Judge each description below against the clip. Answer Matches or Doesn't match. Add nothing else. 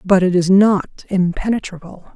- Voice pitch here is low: Doesn't match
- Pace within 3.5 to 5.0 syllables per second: Matches